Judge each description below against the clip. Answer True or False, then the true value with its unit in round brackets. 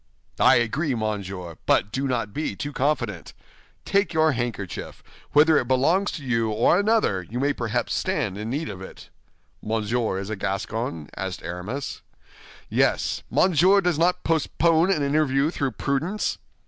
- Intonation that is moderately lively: False (7.0 semitones)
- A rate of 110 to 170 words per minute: True (150 wpm)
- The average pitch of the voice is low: True (130 Hz)